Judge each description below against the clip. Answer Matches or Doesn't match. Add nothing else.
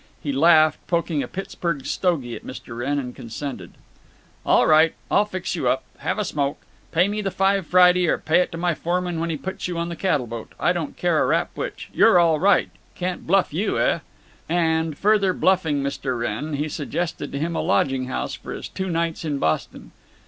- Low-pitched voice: Doesn't match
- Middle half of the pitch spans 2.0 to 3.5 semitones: Doesn't match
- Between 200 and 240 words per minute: Matches